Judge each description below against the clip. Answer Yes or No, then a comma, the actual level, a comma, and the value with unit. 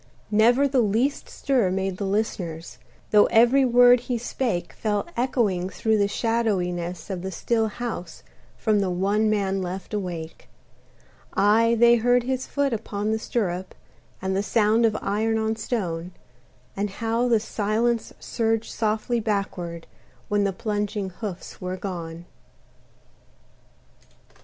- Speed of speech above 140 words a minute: No, slow, 135 wpm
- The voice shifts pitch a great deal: No, average, 3.5 semitones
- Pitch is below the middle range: No, high, 210 Hz